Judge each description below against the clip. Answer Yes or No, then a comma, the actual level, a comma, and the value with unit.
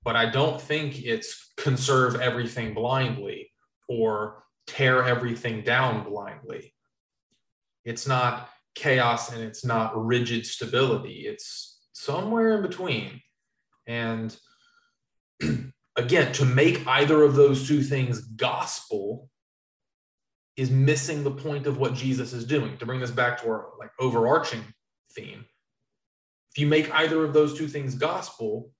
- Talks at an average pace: No, slow, 130 wpm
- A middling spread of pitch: Yes, average, 4.2 semitones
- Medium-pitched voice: No, low, 130 Hz